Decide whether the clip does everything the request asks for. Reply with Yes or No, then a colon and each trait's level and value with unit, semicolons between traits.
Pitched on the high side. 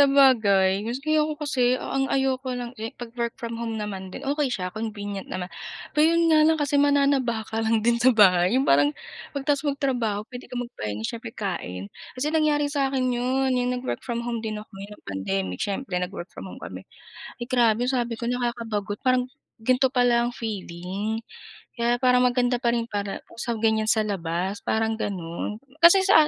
Yes: high, 235 Hz